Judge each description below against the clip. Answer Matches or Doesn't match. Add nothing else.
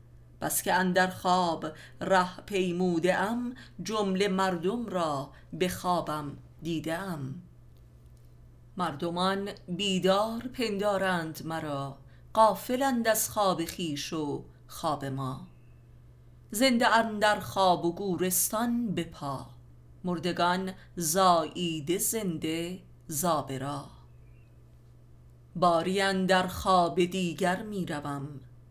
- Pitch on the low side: Doesn't match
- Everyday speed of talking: Doesn't match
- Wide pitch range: Matches